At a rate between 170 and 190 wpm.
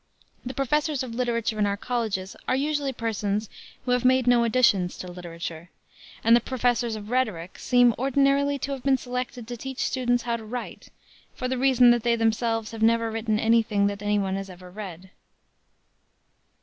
Yes: average, 185 wpm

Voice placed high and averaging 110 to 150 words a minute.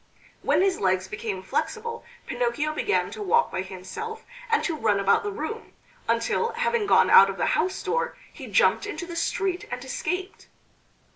No: very high, 380 Hz; average, 170 wpm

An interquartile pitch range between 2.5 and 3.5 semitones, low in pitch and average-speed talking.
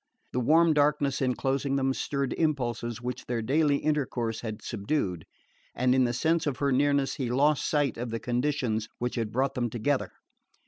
Yes: average, 3.2 semitones; low, 130 Hz; average, 175 wpm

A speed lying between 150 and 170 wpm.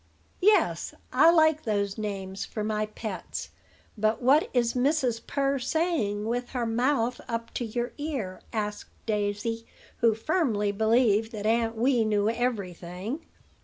No: average, 140 wpm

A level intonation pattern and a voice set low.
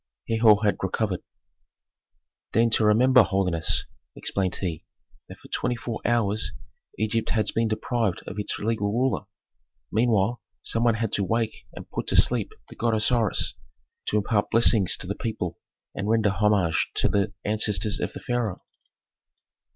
Yes: narrow, 2.3 semitones; low, 110 Hz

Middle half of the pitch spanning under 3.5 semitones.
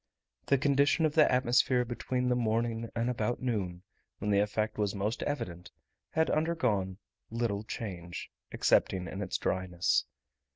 No: average, 4.3 semitones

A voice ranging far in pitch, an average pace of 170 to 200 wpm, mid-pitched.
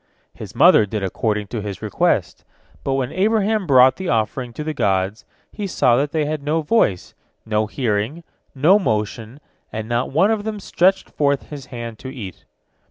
No: wide, 6.9 semitones; average, 175 wpm; low, 130 Hz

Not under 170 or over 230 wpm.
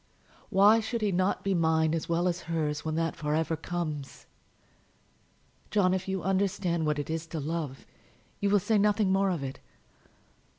Yes: average, 175 wpm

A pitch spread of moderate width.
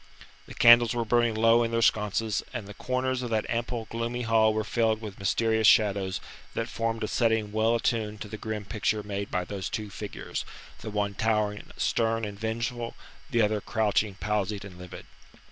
No: narrow, 1.8 semitones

